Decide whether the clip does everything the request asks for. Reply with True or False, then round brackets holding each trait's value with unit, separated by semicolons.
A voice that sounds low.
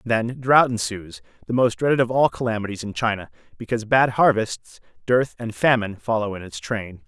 True (115 Hz)